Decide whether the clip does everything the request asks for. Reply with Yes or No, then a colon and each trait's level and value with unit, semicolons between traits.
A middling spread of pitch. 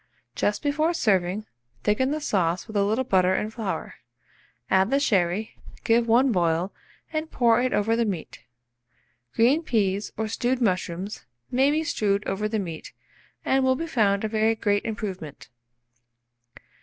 Yes: average, 4.5 semitones